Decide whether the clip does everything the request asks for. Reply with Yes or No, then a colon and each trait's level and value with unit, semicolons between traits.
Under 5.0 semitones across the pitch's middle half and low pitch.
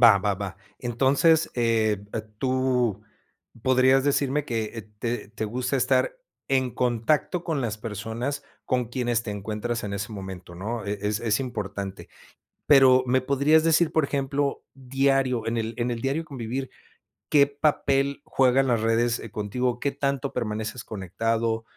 Yes: average, 3.5 semitones; low, 120 Hz